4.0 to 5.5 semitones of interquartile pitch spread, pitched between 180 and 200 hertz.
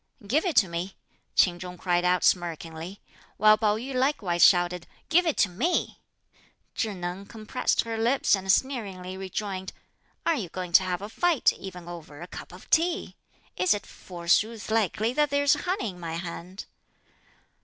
Yes: average, 4.4 semitones; high, 190 Hz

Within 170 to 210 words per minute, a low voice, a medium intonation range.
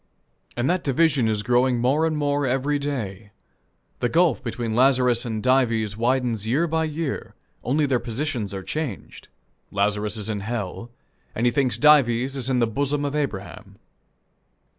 No: average, 160 wpm; low, 125 Hz; average, 4.2 semitones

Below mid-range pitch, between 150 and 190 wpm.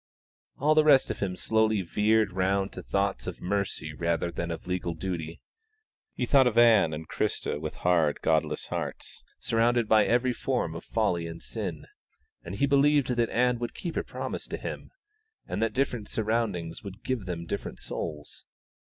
Yes: low, 100 Hz; average, 170 wpm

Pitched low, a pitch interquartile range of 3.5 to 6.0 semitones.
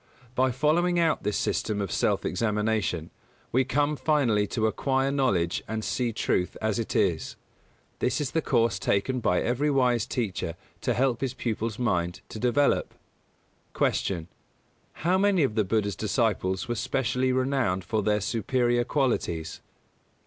Yes: low, 120 Hz; average, 4.2 semitones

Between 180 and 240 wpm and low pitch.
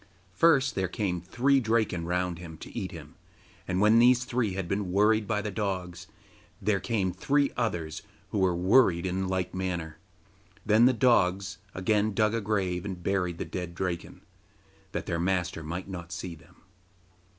No: average, 170 wpm; very low, 95 Hz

